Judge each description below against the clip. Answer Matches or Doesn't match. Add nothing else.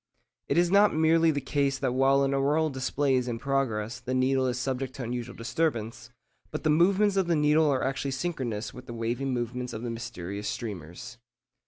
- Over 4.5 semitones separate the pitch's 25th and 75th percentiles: Doesn't match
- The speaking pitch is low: Matches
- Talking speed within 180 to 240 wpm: Matches